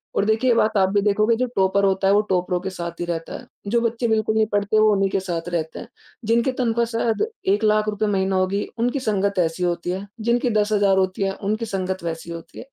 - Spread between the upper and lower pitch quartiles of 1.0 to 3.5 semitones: Yes, narrow, 2.6 semitones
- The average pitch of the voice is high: Yes, high, 200 Hz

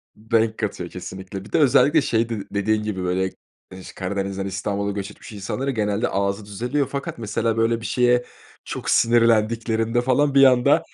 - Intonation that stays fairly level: No, average, 3.4 semitones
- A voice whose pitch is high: No, low, 110 Hz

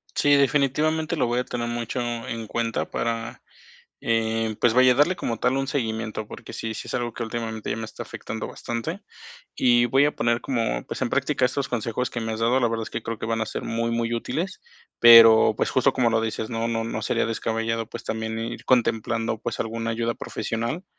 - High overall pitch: No, low, 115 Hz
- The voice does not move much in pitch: Yes, narrow, 1.7 semitones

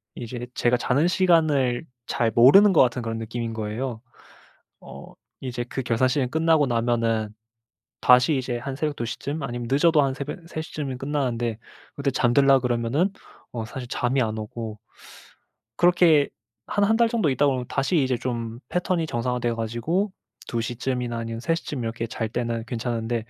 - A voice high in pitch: No, low, 125 Hz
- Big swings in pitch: No, average, 3.7 semitones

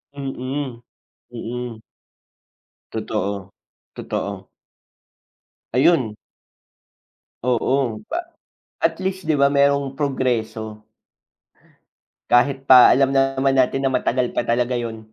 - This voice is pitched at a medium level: No, low, 130 Hz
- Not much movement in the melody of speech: No, average, 3.1 semitones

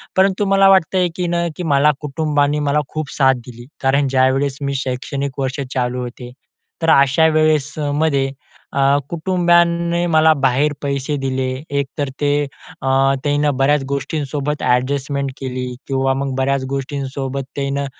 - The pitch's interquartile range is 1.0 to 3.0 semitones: Yes, narrow, 2.4 semitones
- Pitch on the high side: No, medium, 140 Hz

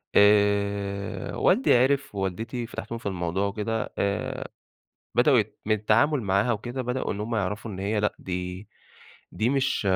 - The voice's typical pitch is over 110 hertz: No, low, 105 Hz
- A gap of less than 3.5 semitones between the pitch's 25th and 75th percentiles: Yes, average, 2.8 semitones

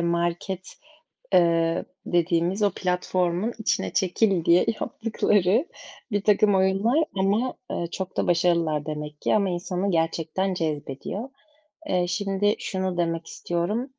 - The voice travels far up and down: No, average, 2.8 semitones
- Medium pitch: Yes, medium, 180 Hz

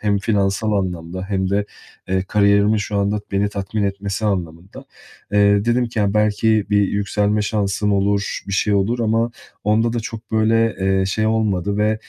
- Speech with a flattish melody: Yes, narrow, 1.7 semitones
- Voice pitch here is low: Yes, low, 100 Hz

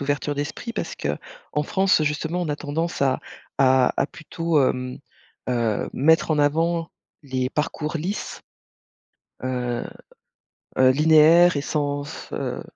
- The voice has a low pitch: No, medium, 150 Hz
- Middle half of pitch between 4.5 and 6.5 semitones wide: No, average, 3.4 semitones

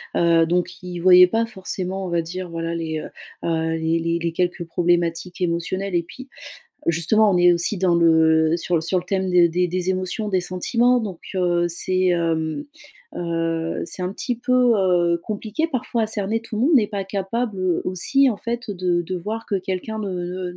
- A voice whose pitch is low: No, medium, 180 Hz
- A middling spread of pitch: Yes, average, 3.1 semitones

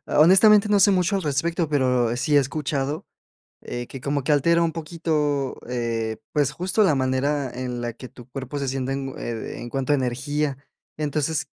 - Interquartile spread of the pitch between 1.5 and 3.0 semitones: No, average, 3.6 semitones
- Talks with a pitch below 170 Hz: Yes, medium, 140 Hz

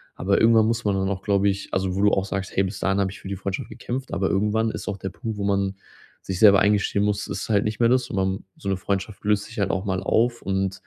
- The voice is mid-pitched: No, low, 100 Hz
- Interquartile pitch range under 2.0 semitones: Yes, narrow, 1.6 semitones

